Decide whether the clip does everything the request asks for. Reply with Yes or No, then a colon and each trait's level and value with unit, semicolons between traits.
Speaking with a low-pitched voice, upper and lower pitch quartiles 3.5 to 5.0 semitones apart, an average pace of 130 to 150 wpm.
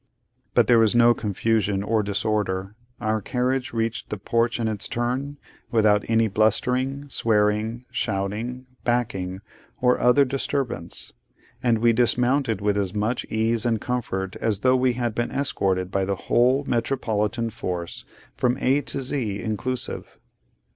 No: low, 115 Hz; average, 3.1 semitones; average, 140 wpm